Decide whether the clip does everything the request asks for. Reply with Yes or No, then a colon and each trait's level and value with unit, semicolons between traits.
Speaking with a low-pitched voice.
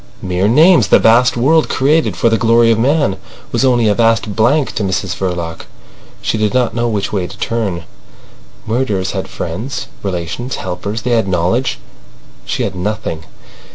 Yes: low, 110 Hz